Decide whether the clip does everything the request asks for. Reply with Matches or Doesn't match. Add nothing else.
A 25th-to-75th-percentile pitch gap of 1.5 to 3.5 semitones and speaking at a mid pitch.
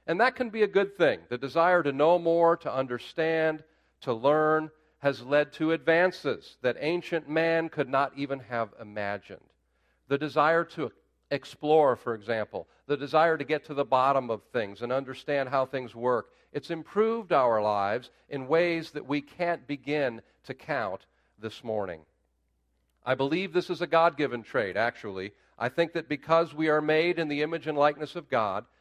Doesn't match